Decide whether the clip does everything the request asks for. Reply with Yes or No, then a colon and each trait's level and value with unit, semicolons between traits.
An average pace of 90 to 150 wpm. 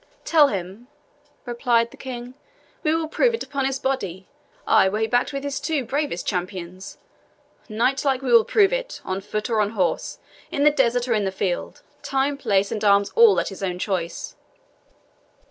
No: average, 180 wpm